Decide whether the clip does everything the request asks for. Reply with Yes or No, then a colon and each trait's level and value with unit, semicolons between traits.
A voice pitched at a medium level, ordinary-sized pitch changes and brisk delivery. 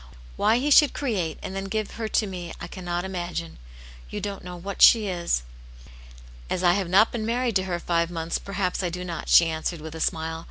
Yes: medium, 180 Hz; average, 3.0 semitones; fast, 215 wpm